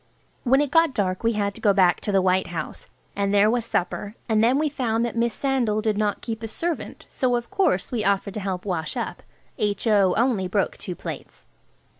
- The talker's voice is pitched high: Yes, high, 215 Hz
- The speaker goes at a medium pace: No, fast, 215 wpm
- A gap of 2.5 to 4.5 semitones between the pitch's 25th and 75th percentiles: Yes, average, 3.4 semitones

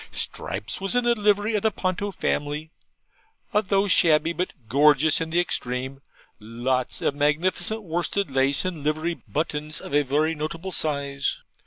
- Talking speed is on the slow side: No, average, 155 wpm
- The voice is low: No, medium, 155 Hz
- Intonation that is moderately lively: Yes, average, 4.6 semitones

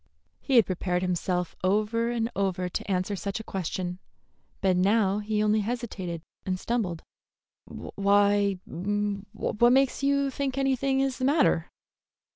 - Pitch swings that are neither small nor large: Yes, average, 4.3 semitones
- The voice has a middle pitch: No, high, 205 Hz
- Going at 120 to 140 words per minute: Yes, slow, 135 wpm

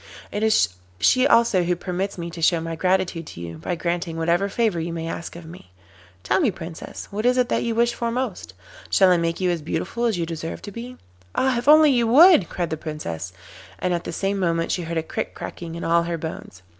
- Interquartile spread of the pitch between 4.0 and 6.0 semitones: Yes, average, 5.3 semitones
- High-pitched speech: No, medium, 175 Hz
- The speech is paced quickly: Yes, fast, 235 wpm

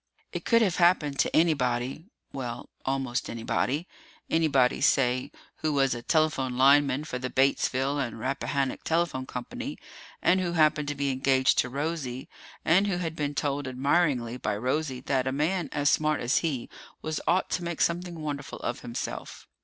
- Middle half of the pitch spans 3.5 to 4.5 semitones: Yes, average, 3.8 semitones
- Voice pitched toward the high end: No, medium, 140 Hz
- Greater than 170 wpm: No, average, 165 wpm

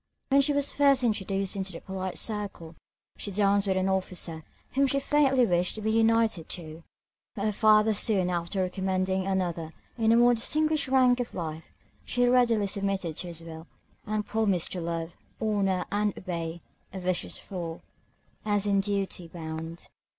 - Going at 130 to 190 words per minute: Yes, average, 165 wpm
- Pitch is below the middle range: No, high, 195 Hz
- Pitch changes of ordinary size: Yes, average, 4.0 semitones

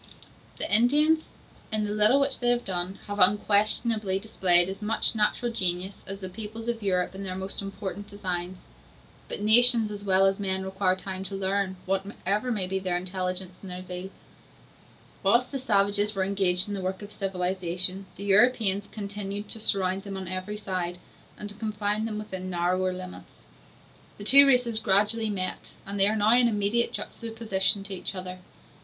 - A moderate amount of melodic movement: No, narrow, 2.3 semitones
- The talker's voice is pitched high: Yes, high, 200 Hz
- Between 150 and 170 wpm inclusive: No, average, 180 wpm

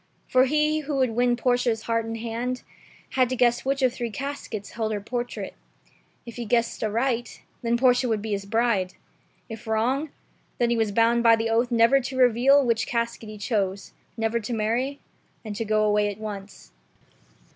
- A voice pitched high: Yes, high, 235 Hz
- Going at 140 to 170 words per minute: No, average, 180 wpm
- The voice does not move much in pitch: Yes, narrow, 2.3 semitones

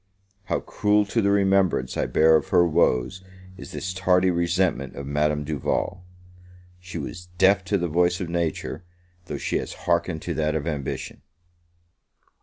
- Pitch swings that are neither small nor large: Yes, average, 3.1 semitones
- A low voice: Yes, very low, 85 Hz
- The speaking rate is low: No, average, 160 wpm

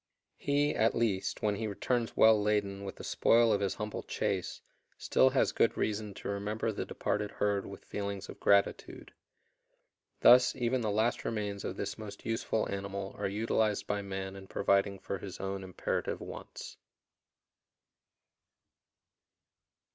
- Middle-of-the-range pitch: No, low, 105 Hz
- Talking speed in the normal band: Yes, average, 145 wpm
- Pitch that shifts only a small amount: Yes, narrow, 2.1 semitones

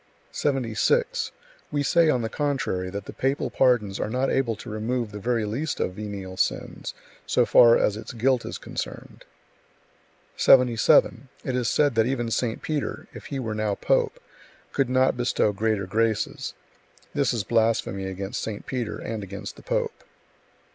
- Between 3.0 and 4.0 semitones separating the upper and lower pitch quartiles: Yes, average, 3.7 semitones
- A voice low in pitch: Yes, low, 115 Hz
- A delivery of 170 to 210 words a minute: No, average, 160 wpm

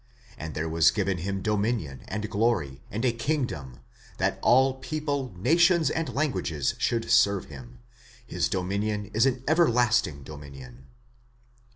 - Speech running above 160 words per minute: No, slow, 135 wpm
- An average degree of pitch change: No, wide, 8.6 semitones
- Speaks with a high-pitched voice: No, low, 105 Hz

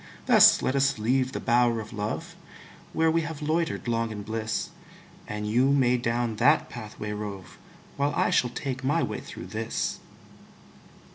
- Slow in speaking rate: No, average, 160 wpm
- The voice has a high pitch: No, low, 120 Hz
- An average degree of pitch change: Yes, average, 4.1 semitones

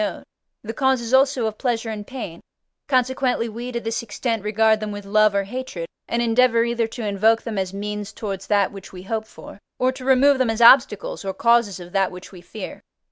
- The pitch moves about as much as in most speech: Yes, average, 3.2 semitones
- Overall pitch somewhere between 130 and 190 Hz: No, high, 225 Hz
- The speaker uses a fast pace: Yes, fast, 210 wpm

